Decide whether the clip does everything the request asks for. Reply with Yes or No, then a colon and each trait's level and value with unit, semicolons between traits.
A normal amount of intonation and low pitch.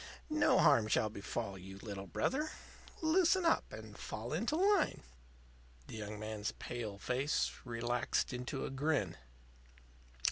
No: wide, 7.1 semitones; low, 120 Hz